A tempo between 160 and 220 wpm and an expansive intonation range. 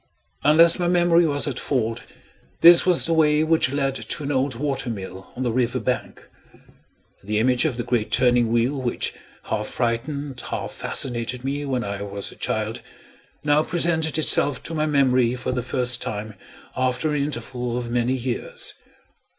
No: average, 170 wpm; average, 3.8 semitones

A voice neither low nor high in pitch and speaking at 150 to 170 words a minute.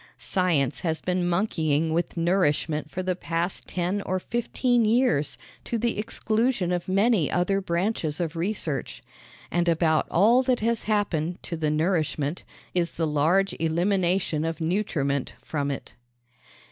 No: medium, 175 Hz; average, 140 wpm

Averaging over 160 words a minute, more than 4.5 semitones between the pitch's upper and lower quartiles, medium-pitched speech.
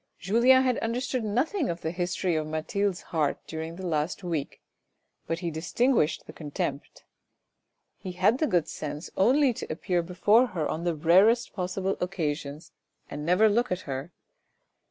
No: average, 155 wpm; wide, 5.5 semitones; medium, 180 Hz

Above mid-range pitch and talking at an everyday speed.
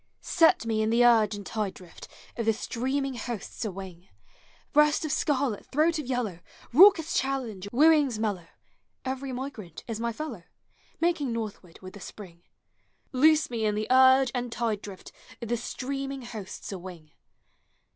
Yes: high, 235 Hz; average, 160 wpm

